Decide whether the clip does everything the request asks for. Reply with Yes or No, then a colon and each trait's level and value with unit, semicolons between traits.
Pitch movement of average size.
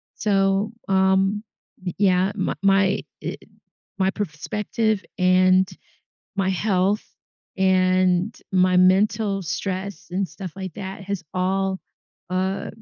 No: narrow, 1.3 semitones